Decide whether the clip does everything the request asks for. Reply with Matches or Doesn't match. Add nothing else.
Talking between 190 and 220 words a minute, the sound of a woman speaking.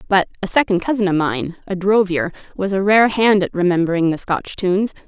Matches